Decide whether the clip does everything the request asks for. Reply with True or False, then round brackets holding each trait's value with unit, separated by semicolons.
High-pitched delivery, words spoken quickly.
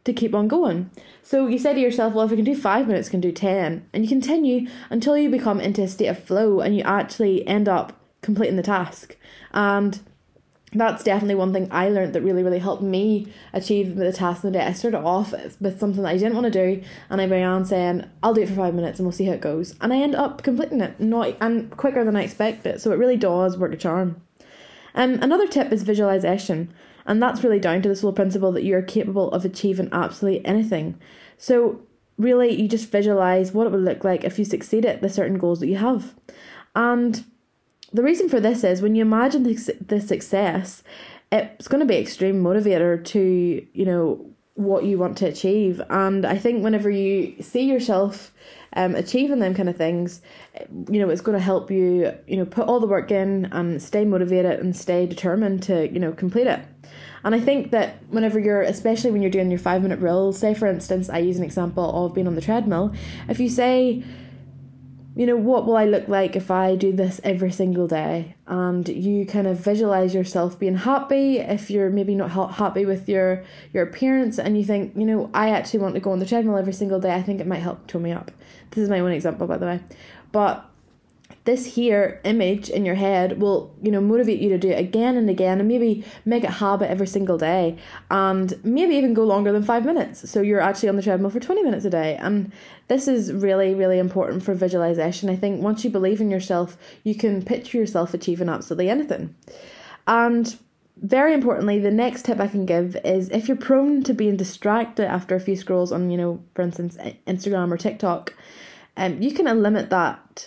True (195 Hz; 215 wpm)